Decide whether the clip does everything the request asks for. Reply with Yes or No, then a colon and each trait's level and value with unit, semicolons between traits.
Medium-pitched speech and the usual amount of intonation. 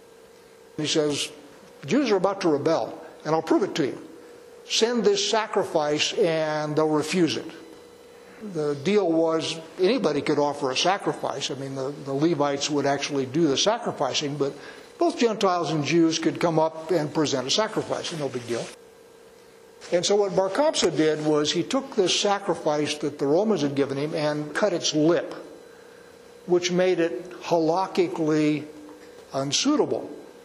No: medium, 165 Hz; wide, 6.4 semitones